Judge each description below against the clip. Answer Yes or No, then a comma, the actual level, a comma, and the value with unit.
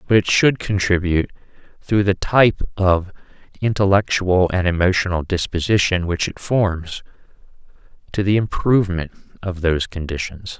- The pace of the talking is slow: Yes, slow, 120 wpm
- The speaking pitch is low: Yes, very low, 95 Hz